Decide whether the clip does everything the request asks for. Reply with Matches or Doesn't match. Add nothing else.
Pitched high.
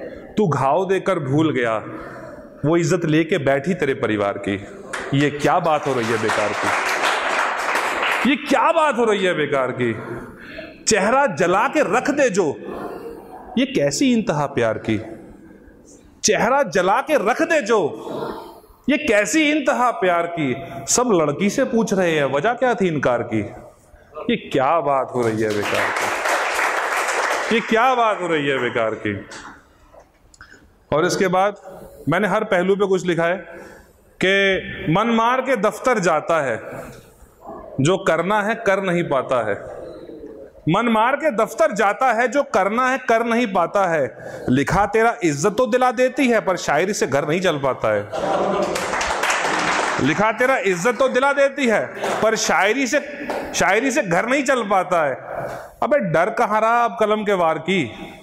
Matches